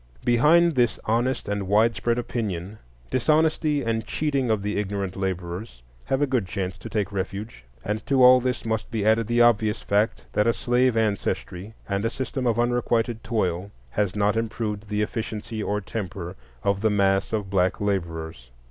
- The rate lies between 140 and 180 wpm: Yes, average, 170 wpm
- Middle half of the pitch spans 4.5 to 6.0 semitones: No, average, 3.2 semitones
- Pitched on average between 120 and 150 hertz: No, low, 110 Hz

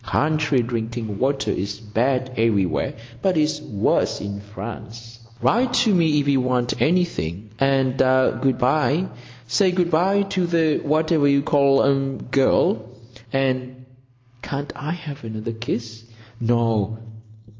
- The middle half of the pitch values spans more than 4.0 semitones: Yes, average, 4.5 semitones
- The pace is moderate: No, slow, 125 wpm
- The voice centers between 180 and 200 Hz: No, low, 130 Hz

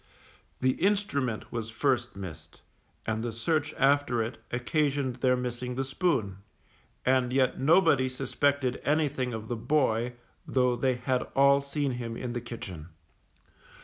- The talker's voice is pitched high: No, low, 125 Hz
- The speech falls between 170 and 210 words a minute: No, average, 140 wpm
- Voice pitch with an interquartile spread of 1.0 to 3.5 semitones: Yes, average, 2.8 semitones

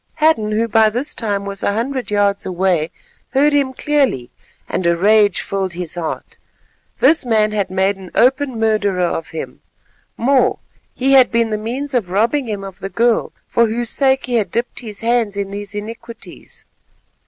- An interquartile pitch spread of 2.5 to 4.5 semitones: Yes, average, 3.8 semitones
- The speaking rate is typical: Yes, average, 175 wpm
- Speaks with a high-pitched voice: Yes, high, 220 Hz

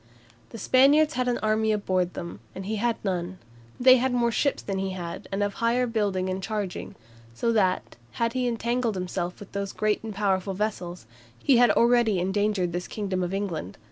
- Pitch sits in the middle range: No, high, 205 Hz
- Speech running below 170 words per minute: No, average, 190 wpm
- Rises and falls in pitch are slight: No, average, 4.0 semitones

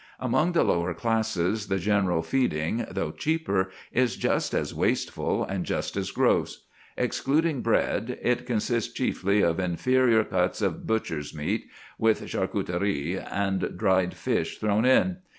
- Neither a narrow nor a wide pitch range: Yes, average, 4.9 semitones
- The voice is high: No, low, 105 Hz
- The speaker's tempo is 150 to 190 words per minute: No, slow, 135 wpm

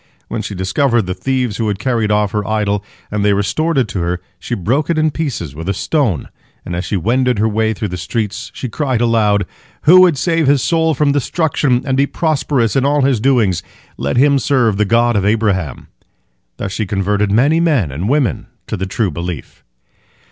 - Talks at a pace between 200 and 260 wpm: Yes, fast, 205 wpm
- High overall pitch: No, low, 115 Hz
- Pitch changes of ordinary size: No, wide, 5.7 semitones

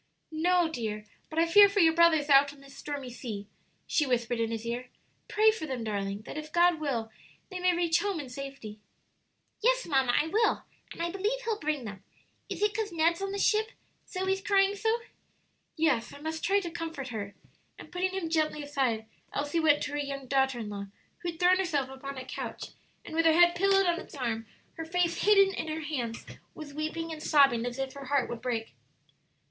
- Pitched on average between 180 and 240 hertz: No, very high, 310 Hz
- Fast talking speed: Yes, fast, 210 wpm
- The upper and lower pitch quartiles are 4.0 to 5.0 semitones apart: No, wide, 5.4 semitones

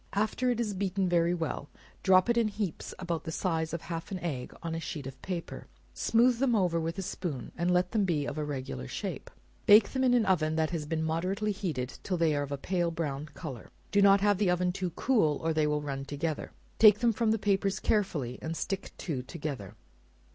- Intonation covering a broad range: No, average, 4.5 semitones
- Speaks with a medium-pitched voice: Yes, medium, 175 Hz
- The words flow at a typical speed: No, fast, 225 wpm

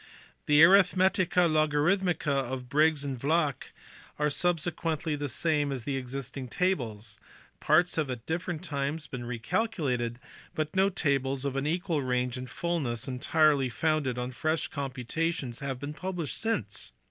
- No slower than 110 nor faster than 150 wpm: Yes, average, 145 wpm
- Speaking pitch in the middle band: Yes, medium, 145 Hz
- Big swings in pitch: No, average, 4.2 semitones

